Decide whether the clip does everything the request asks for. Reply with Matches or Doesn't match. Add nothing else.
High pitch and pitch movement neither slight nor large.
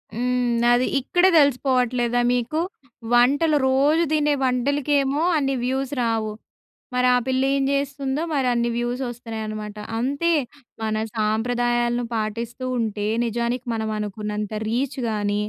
Matches